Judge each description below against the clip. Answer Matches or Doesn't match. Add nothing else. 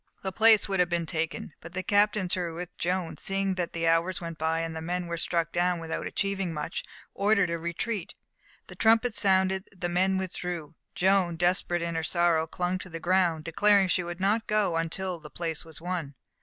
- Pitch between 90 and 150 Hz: Doesn't match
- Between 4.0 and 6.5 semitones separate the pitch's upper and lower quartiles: Doesn't match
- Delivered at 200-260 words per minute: Matches